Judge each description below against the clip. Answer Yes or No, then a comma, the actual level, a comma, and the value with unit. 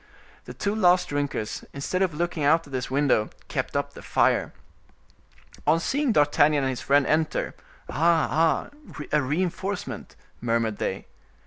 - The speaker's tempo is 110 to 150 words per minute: Yes, average, 140 wpm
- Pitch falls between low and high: Yes, medium, 150 Hz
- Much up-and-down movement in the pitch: No, average, 3.8 semitones